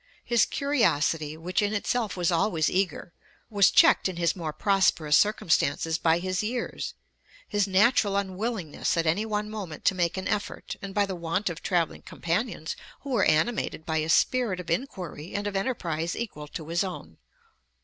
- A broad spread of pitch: No, average, 4.1 semitones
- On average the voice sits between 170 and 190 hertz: Yes, medium, 185 Hz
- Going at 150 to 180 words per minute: Yes, average, 170 wpm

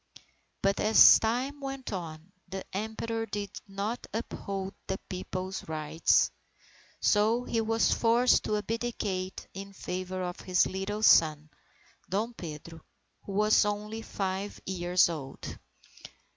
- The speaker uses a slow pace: Yes, slow, 120 wpm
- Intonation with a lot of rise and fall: No, average, 3.2 semitones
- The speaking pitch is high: Yes, high, 195 Hz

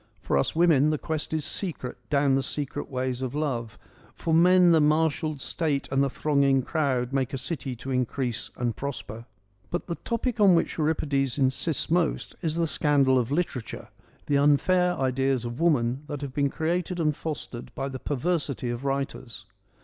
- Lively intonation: No, average, 3.5 semitones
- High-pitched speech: No, medium, 140 Hz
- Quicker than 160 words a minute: Yes, average, 175 wpm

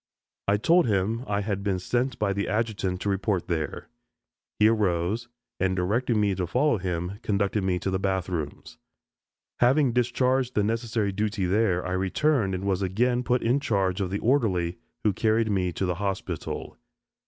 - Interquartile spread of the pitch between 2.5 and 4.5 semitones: Yes, average, 3.6 semitones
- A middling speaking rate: Yes, average, 175 wpm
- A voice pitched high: No, low, 100 Hz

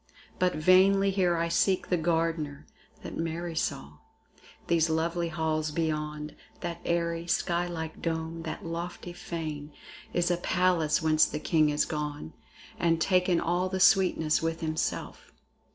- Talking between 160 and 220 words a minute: No, average, 145 wpm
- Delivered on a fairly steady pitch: Yes, narrow, 1.9 semitones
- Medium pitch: Yes, medium, 165 Hz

